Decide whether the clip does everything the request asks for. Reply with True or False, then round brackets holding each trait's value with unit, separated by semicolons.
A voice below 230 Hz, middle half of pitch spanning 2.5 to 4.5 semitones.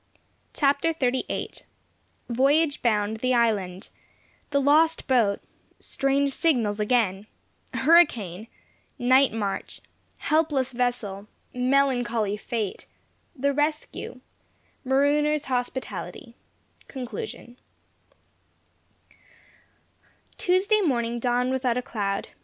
False (250 Hz; 3.8 semitones)